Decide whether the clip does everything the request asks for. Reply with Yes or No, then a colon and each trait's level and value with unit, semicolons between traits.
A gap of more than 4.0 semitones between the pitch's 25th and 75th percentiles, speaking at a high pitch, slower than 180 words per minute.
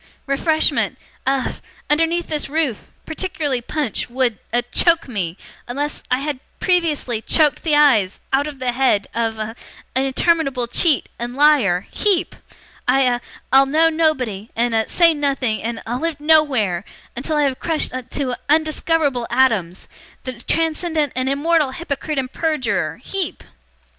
Yes: average, 4.5 semitones; very high, 275 Hz; average, 145 wpm